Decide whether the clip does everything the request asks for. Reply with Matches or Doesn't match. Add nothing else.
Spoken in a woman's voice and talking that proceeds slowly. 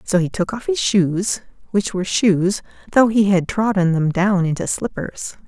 Doesn't match